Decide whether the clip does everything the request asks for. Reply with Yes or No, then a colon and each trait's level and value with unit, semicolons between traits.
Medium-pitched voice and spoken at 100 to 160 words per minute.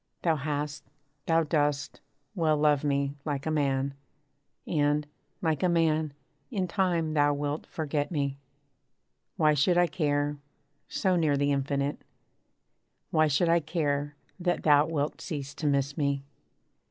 Yes: medium, 150 Hz; average, 140 wpm